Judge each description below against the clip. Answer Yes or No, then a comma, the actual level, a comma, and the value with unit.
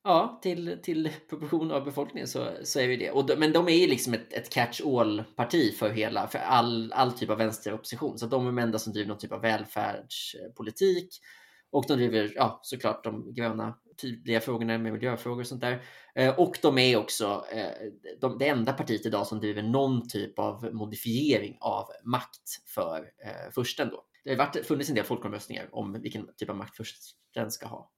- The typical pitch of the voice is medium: No, low, 120 Hz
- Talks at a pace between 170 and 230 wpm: Yes, fast, 195 wpm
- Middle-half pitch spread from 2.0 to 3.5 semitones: No, average, 4.0 semitones